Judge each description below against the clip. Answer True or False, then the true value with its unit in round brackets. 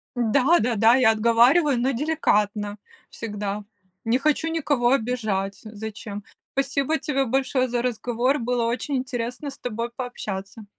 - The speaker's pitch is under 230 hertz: False (240 Hz)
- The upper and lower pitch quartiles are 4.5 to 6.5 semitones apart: False (3.6 semitones)